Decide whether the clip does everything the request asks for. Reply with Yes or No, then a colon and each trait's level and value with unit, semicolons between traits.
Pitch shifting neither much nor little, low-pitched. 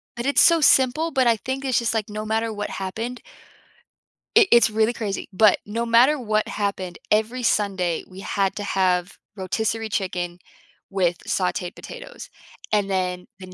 No: average, 3.7 semitones; high, 215 Hz